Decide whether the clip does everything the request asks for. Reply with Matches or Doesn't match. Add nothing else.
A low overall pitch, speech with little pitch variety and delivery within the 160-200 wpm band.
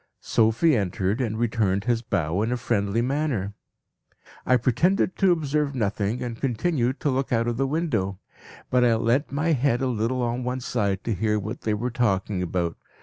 Doesn't match